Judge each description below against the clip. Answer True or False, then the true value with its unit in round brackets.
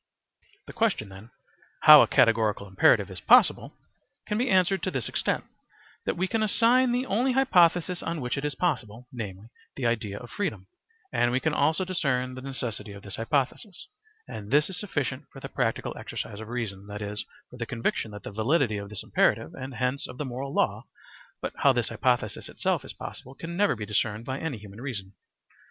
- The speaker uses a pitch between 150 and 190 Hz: False (130 Hz)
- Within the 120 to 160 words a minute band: False (195 wpm)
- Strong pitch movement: True (8.0 semitones)